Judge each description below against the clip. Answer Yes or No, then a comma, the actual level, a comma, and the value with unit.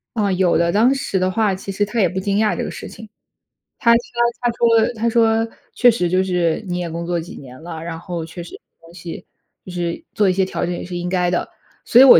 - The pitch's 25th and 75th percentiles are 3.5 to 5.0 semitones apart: Yes, average, 4.2 semitones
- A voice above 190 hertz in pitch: No, medium, 185 Hz